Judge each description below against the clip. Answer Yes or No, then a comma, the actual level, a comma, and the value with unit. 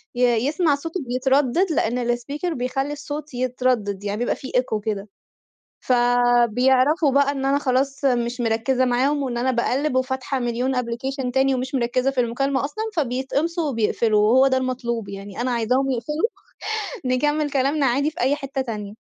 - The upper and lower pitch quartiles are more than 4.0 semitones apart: No, narrow, 2.5 semitones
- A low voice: No, very high, 255 Hz